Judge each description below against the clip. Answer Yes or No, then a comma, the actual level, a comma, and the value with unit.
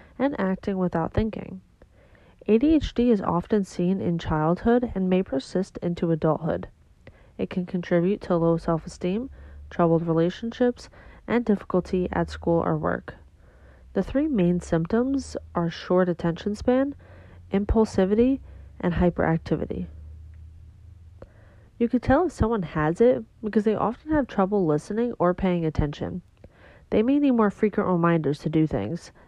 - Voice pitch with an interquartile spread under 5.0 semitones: No, average, 5.3 semitones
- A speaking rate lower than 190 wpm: Yes, slow, 135 wpm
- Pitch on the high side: No, medium, 180 Hz